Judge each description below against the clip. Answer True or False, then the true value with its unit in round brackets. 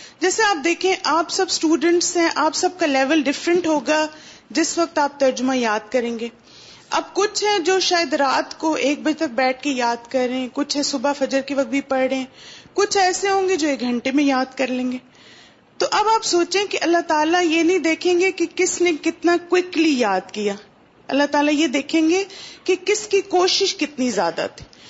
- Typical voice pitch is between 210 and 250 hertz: False (315 Hz)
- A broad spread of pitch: False (5.0 semitones)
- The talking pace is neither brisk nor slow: False (200 wpm)